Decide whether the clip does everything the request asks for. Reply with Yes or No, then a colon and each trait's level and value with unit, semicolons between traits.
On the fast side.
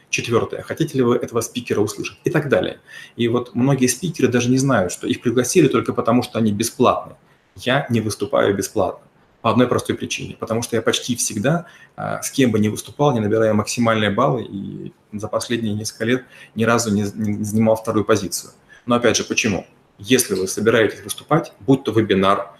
Yes: fast, 185 wpm